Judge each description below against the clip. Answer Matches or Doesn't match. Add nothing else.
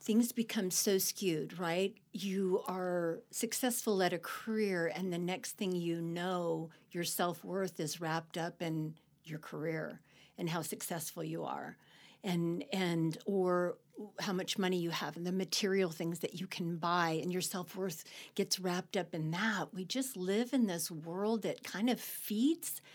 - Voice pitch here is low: Doesn't match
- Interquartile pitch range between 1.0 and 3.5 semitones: Matches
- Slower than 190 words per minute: Matches